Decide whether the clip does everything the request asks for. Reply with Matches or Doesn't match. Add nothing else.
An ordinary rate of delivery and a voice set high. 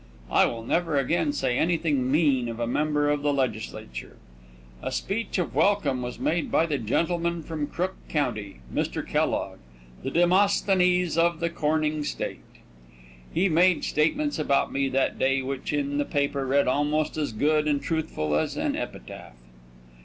Doesn't match